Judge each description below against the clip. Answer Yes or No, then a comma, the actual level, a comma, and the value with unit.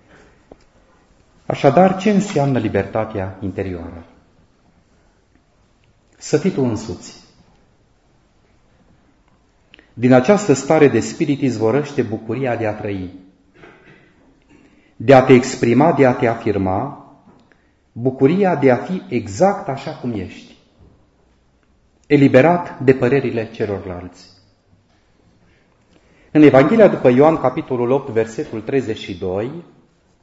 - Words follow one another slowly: Yes, slow, 95 wpm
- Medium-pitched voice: No, low, 120 Hz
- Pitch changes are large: Yes, wide, 6.1 semitones